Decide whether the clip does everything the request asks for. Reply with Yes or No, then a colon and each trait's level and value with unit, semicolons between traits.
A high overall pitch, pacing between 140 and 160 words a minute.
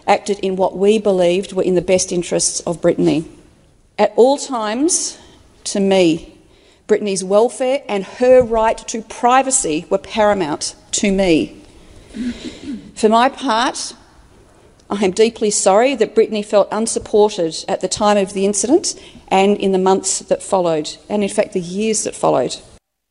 Yes: high, 205 Hz; average, 150 wpm